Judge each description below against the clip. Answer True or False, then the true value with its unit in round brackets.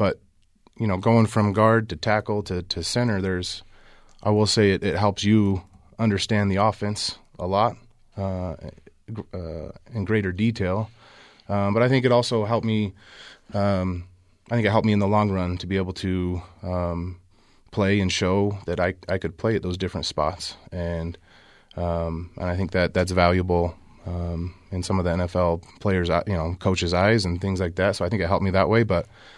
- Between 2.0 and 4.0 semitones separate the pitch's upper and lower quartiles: True (2.8 semitones)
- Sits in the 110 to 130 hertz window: False (95 Hz)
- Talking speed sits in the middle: True (195 wpm)